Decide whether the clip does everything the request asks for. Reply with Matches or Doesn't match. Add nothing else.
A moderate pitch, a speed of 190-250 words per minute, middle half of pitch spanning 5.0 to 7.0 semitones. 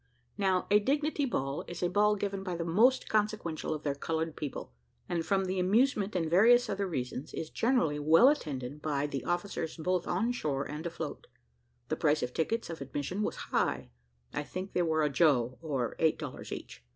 Matches